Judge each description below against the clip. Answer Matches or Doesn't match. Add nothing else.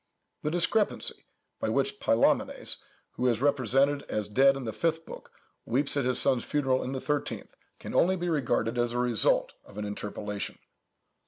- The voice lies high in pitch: Doesn't match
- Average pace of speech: Matches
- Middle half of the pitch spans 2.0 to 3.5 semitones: Doesn't match